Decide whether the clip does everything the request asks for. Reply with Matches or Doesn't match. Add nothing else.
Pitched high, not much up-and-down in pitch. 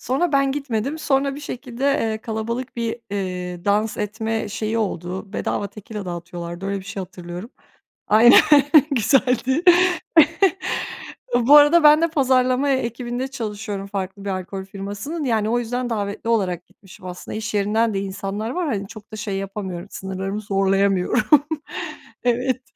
Doesn't match